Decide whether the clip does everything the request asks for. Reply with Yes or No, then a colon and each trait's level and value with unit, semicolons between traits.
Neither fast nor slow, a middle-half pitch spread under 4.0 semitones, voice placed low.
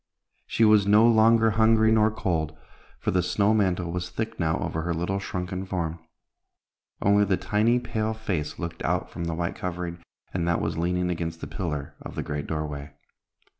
No: average, 180 wpm; average, 4.4 semitones; very low, 90 Hz